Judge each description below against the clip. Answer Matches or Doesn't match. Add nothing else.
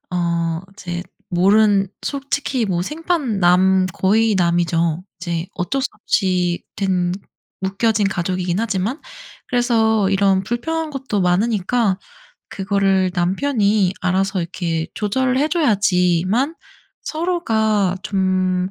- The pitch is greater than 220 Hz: Doesn't match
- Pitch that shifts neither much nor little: Matches